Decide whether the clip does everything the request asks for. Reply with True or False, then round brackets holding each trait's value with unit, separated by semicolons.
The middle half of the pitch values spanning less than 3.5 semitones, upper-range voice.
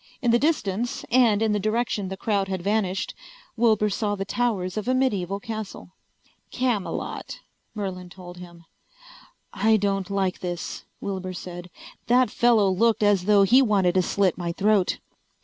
True (3.1 semitones; 200 Hz)